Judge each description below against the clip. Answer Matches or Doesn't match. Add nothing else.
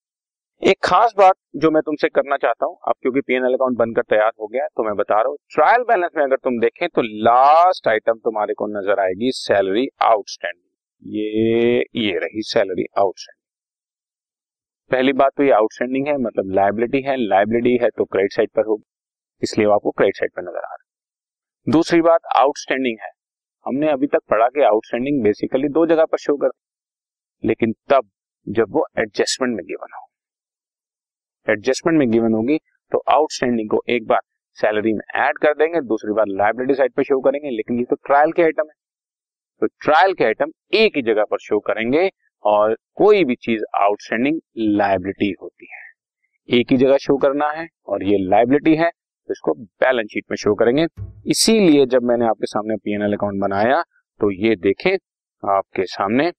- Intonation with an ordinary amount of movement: Doesn't match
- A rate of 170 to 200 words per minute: Matches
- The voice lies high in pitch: Doesn't match